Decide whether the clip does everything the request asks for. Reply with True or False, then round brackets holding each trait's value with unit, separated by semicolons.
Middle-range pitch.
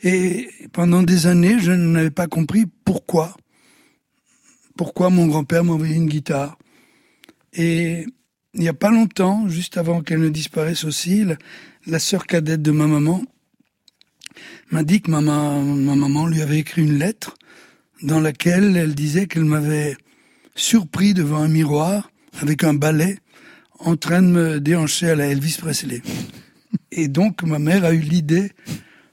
True (165 Hz)